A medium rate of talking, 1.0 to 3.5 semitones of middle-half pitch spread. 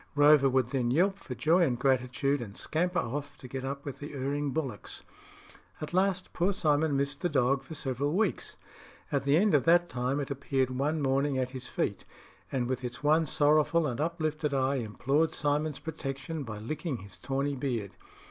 Yes: average, 185 wpm; average, 2.9 semitones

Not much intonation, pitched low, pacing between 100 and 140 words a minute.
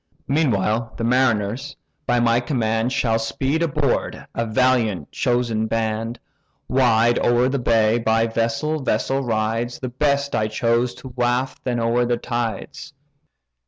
Yes: narrow, 2.2 semitones; low, 120 Hz; slow, 135 wpm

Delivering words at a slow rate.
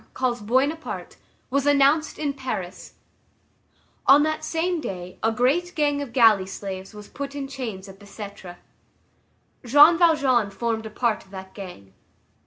No: average, 150 wpm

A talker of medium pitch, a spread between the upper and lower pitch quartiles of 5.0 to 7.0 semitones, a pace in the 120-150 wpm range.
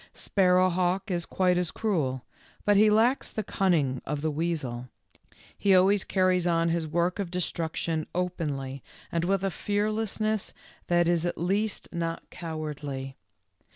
No: medium, 175 Hz; average, 3.5 semitones; average, 140 wpm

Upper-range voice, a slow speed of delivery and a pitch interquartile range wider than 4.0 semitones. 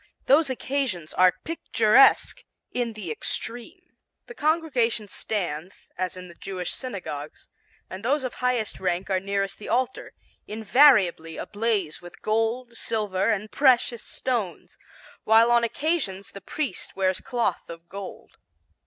Yes: high, 215 Hz; slow, 130 wpm; average, 5.1 semitones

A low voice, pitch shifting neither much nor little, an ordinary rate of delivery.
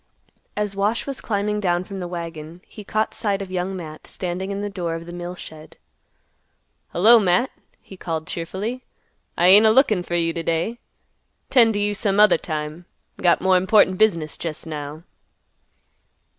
No: medium, 185 Hz; average, 3.6 semitones; average, 170 wpm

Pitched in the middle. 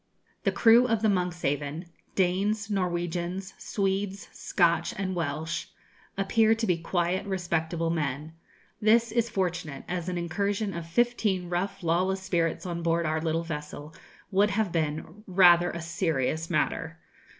Yes: medium, 175 Hz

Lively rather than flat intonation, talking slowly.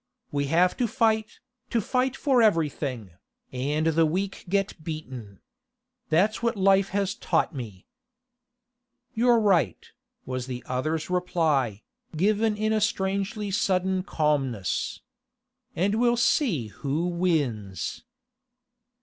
Yes: wide, 7.0 semitones; slow, 115 wpm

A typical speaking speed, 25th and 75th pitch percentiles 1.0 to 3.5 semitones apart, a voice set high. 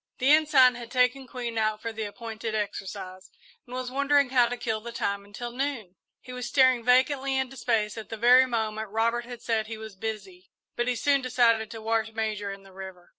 No: fast, 210 wpm; average, 2.7 semitones; high, 230 Hz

